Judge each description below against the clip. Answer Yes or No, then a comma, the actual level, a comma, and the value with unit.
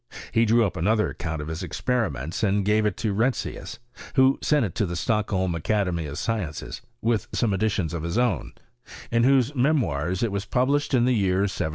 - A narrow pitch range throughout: No, average, 5.1 semitones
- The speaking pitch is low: Yes, low, 105 Hz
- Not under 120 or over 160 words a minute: No, average, 195 wpm